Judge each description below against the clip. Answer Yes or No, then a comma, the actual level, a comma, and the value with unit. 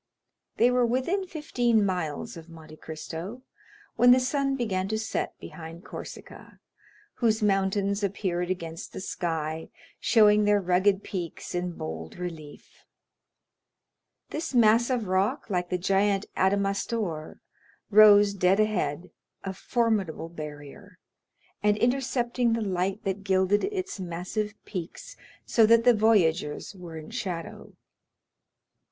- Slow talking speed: Yes, slow, 120 wpm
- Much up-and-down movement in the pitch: No, average, 4.3 semitones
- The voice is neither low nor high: No, high, 200 Hz